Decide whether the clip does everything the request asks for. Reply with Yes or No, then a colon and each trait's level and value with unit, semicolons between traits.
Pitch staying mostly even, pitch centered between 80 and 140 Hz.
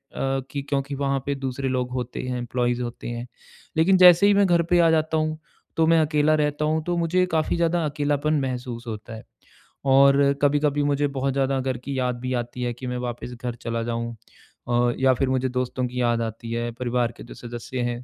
No: average, 3.5 semitones; low, 135 Hz